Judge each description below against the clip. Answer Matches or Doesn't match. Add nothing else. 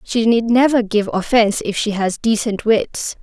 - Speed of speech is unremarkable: Matches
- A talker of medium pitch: Doesn't match